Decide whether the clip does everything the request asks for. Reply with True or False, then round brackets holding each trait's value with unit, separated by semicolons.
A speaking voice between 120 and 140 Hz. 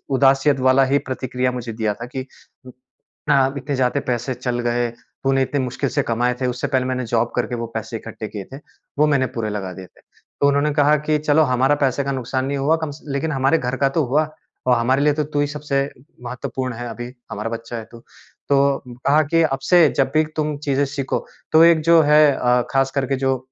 True (135 Hz)